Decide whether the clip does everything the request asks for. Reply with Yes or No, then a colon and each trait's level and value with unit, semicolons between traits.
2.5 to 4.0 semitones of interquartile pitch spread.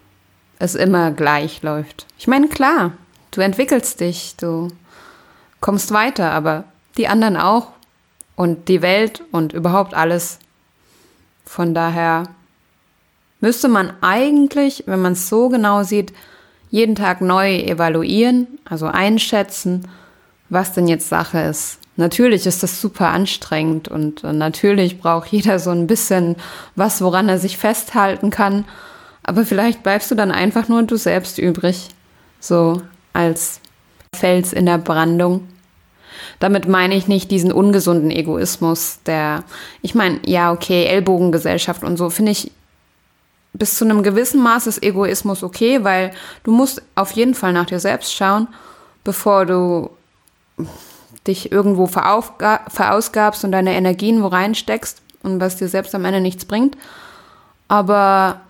Yes: average, 3.4 semitones